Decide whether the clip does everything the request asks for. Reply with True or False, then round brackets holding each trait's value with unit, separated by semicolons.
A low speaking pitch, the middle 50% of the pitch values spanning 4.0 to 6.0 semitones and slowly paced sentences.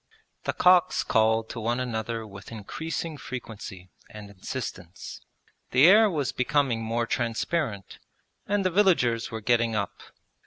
True (115 Hz; 5.2 semitones; 130 wpm)